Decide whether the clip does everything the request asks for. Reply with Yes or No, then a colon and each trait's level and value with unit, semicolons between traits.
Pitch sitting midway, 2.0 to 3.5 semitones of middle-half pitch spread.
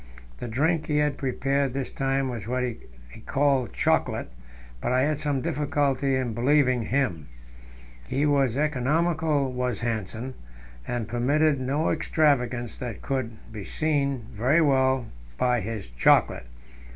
No: low, 130 Hz; average, 2.9 semitones